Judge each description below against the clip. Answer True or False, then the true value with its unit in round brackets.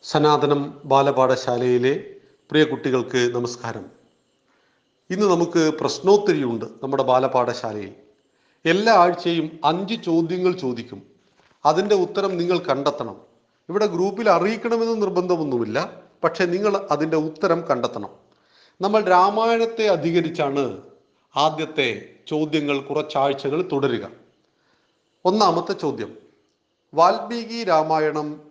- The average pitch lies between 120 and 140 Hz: False (155 Hz)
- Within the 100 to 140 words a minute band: False (80 wpm)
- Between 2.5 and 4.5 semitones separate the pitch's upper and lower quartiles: False (5.4 semitones)